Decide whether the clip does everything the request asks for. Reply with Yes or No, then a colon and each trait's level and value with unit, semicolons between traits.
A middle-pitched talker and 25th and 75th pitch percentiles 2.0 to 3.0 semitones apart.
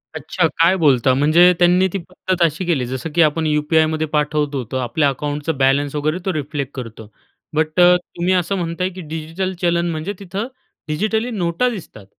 No: medium, 160 Hz; average, 3.4 semitones